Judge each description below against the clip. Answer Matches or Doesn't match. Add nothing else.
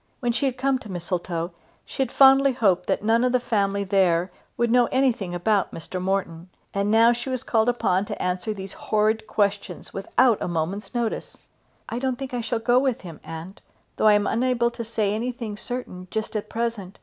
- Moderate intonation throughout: Matches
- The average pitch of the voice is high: Matches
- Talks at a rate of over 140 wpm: Matches